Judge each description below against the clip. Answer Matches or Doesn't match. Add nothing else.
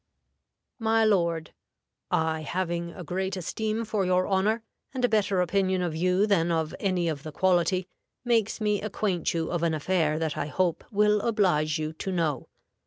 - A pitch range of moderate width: Matches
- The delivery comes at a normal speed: Matches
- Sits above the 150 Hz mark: Matches